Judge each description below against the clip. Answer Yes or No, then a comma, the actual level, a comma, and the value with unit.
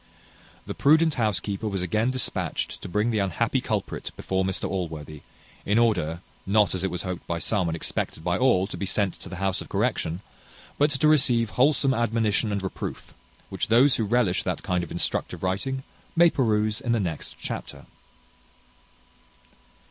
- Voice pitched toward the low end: Yes, low, 105 Hz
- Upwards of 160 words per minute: Yes, average, 170 wpm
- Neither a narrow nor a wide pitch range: Yes, average, 4.5 semitones